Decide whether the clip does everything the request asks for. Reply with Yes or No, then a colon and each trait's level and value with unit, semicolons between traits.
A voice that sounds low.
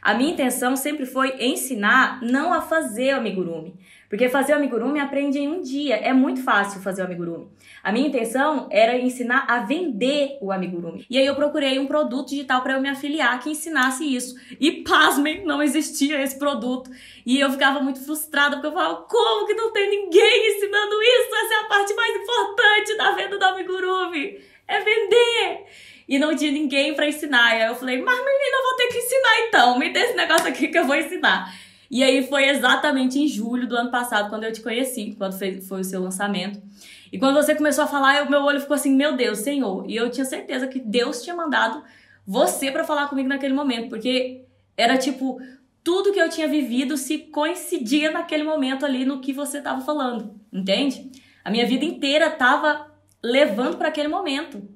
No: very high, 280 Hz